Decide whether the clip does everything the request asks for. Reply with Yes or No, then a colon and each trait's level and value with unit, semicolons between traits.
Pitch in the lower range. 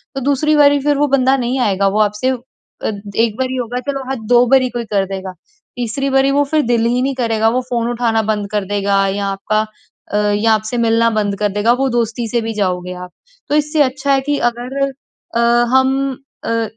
No: high, 240 Hz